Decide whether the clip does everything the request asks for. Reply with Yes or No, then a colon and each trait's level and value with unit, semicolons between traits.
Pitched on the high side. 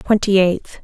Yes: high, 195 Hz